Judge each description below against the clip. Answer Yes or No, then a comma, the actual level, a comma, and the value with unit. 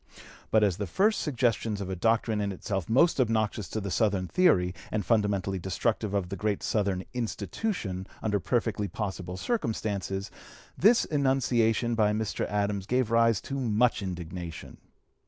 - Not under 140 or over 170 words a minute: Yes, average, 150 wpm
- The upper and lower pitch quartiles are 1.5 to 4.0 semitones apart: Yes, average, 3.2 semitones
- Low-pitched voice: Yes, low, 105 Hz